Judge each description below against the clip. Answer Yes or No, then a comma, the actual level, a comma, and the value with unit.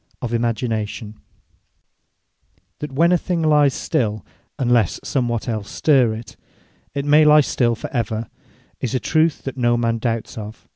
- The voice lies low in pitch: Yes, low, 120 Hz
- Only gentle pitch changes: No, average, 4.1 semitones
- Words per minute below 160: Yes, average, 150 wpm